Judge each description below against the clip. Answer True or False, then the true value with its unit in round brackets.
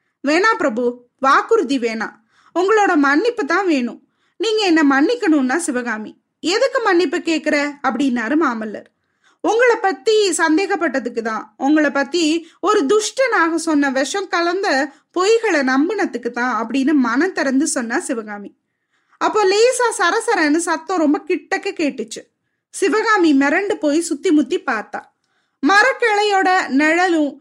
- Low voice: False (320 Hz)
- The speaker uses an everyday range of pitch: False (5.9 semitones)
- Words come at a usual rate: True (110 wpm)